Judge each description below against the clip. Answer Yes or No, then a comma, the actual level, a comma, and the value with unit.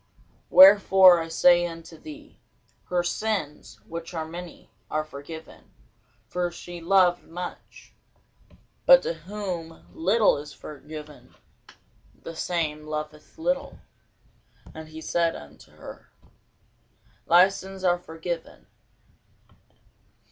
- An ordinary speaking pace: No, slow, 105 wpm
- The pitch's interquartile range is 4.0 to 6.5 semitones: No, average, 2.8 semitones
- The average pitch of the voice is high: No, medium, 170 Hz